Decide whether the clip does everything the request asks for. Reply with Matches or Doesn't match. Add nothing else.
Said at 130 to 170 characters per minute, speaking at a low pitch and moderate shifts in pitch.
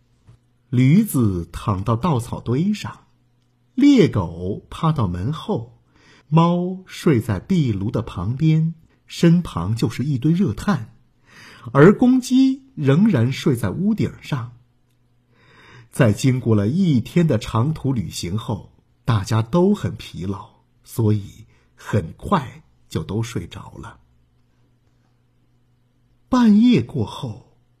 Doesn't match